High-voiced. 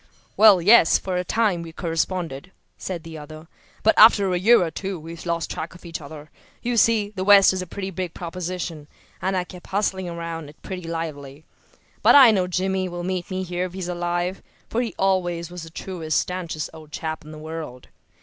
No: medium, 175 Hz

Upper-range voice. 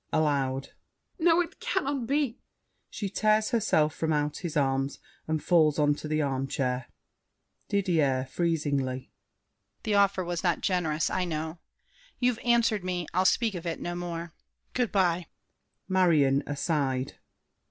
No: medium, 170 Hz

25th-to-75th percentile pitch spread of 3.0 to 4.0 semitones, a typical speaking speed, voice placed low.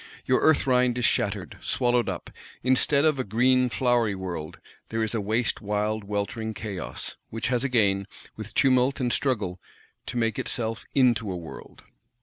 Yes: average, 3.3 semitones; average, 155 wpm; low, 115 Hz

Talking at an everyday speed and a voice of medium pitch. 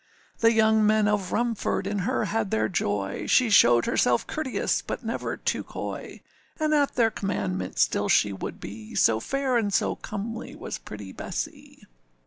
No: average, 165 wpm; high, 210 Hz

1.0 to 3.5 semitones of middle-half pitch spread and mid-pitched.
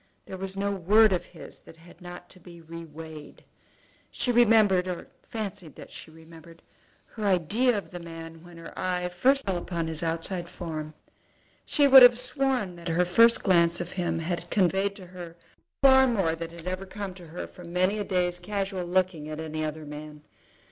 Yes: average, 3.2 semitones; medium, 180 Hz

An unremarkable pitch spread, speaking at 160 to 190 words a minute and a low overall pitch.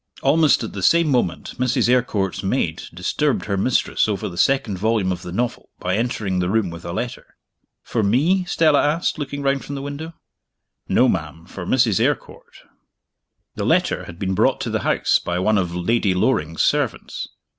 No: wide, 6.9 semitones; average, 180 wpm; low, 110 Hz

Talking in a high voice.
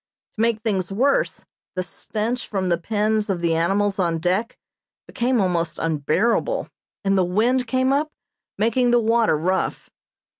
Yes: high, 210 Hz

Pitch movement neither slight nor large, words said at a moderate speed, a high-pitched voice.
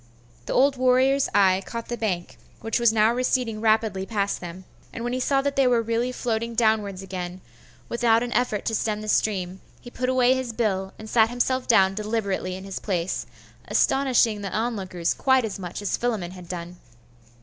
Yes: average, 4.1 semitones; average, 190 wpm; high, 220 Hz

